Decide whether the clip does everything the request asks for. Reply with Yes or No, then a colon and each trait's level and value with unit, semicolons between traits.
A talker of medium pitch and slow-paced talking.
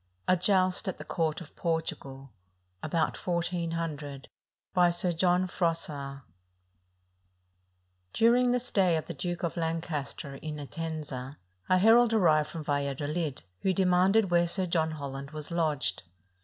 Yes: medium, 165 Hz; slow, 130 wpm